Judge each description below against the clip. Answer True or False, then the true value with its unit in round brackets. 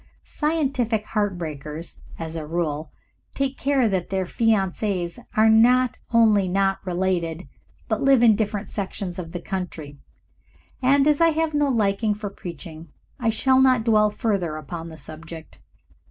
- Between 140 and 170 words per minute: True (150 wpm)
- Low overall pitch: False (200 Hz)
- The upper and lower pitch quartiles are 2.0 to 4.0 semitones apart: False (5.6 semitones)